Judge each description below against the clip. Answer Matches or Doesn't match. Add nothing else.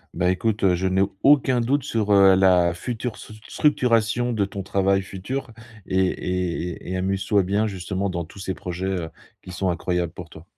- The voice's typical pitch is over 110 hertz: Doesn't match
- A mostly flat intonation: Doesn't match